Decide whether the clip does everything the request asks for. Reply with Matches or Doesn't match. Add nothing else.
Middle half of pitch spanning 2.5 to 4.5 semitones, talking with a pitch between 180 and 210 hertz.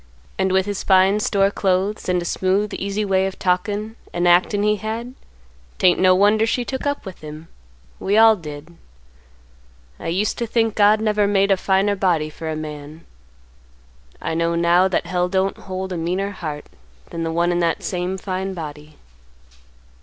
Matches